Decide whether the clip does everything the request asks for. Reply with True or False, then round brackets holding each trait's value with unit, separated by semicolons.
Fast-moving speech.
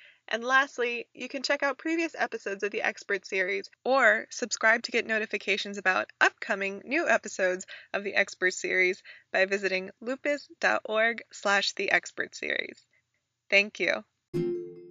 False (135 wpm)